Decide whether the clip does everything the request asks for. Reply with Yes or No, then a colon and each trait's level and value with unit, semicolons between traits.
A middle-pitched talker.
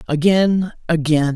Yes: medium, 165 Hz